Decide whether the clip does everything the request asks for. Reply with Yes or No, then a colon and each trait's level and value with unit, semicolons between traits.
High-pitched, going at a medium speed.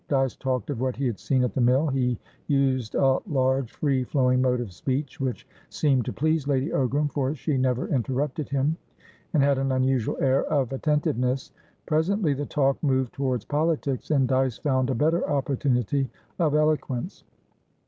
No: low, 135 Hz; average, 170 wpm